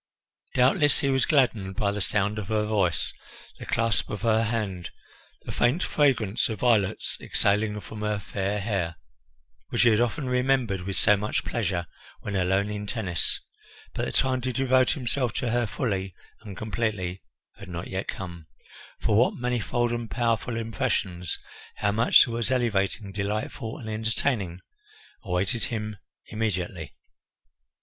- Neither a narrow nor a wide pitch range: Yes, average, 3.6 semitones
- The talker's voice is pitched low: Yes, low, 110 Hz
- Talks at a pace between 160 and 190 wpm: No, average, 150 wpm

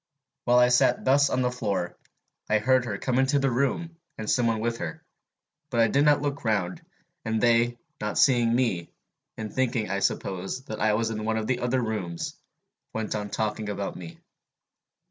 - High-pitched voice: No, low, 115 Hz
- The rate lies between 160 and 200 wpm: Yes, average, 190 wpm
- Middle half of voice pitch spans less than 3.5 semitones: Yes, average, 3.1 semitones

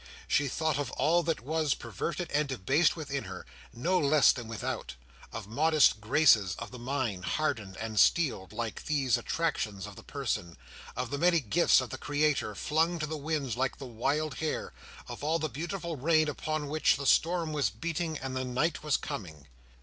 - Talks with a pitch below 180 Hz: Yes, medium, 140 Hz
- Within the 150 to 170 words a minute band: No, average, 185 wpm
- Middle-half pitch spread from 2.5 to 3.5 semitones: No, average, 5.1 semitones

